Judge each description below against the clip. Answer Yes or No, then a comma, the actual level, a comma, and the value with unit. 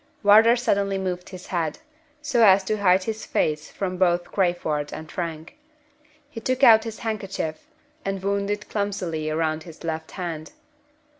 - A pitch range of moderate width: Yes, average, 4.0 semitones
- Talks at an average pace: Yes, average, 155 wpm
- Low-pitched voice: No, high, 190 Hz